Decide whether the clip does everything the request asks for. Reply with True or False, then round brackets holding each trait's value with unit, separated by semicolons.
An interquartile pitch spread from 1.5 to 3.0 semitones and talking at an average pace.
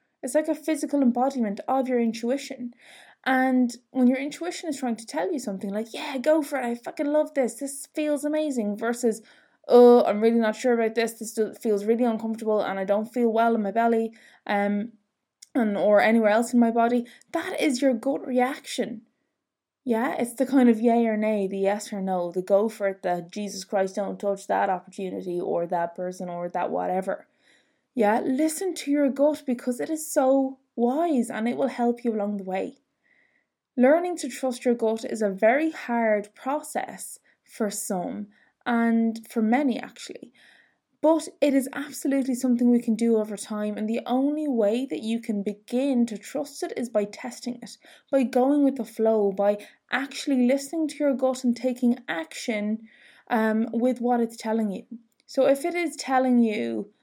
False (4.0 semitones; 185 wpm)